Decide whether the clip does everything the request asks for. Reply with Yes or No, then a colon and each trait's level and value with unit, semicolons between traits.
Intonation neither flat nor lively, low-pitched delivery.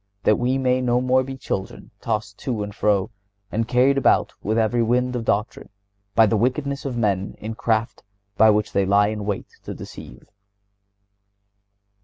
Yes: average, 3.4 semitones; low, 115 Hz